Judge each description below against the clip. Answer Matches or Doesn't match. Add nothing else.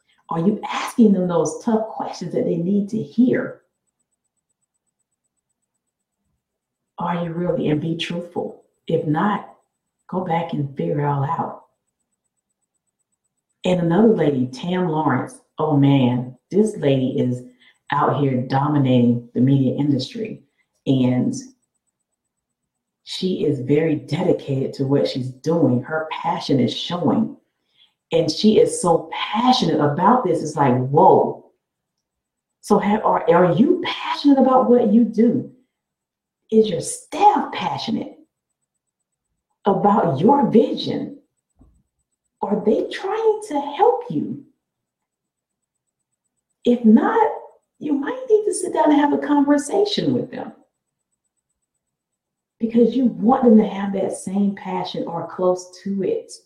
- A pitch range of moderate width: Doesn't match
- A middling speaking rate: Doesn't match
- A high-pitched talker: Matches